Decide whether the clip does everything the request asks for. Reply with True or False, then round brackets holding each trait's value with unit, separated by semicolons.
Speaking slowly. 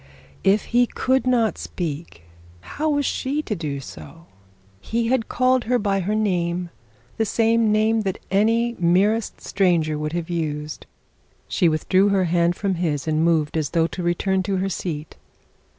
False (165 wpm)